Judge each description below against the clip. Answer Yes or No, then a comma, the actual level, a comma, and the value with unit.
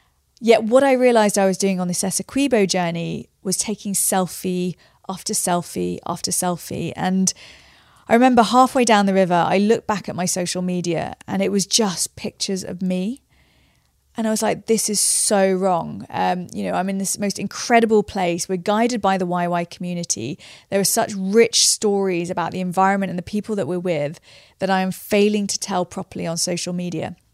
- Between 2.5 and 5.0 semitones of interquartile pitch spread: Yes, average, 2.8 semitones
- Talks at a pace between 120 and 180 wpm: No, average, 190 wpm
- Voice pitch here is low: No, high, 190 Hz